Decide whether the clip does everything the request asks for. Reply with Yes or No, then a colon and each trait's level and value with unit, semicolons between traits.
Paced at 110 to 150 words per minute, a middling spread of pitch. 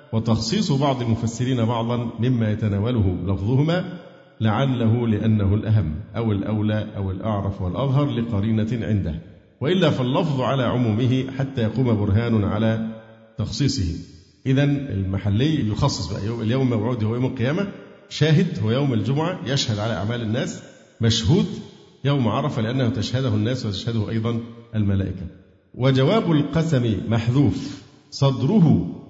Yes: average, 115 wpm; average, 4.2 semitones